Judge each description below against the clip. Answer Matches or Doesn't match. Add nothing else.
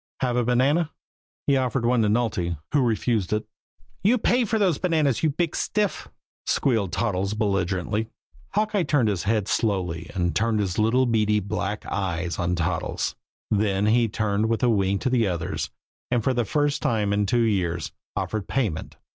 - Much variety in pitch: Doesn't match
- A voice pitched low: Matches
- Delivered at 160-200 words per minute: Matches